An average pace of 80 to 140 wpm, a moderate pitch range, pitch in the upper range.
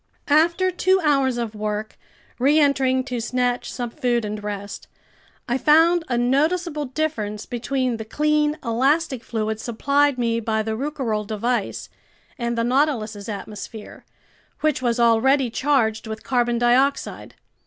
Yes: slow, 135 wpm; average, 4.3 semitones; high, 245 Hz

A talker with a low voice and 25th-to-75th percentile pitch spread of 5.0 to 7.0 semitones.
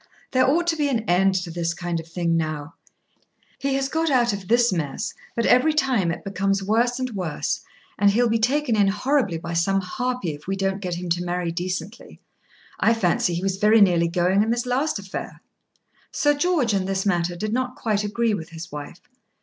No: high, 195 Hz; wide, 5.6 semitones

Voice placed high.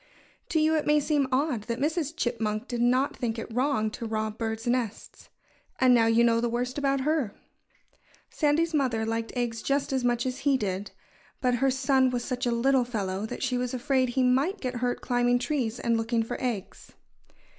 Yes: high, 245 Hz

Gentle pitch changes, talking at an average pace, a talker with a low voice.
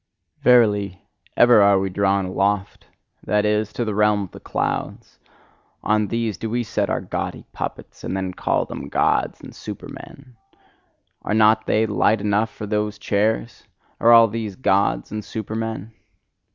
Yes: narrow, 1.9 semitones; average, 150 wpm; low, 105 Hz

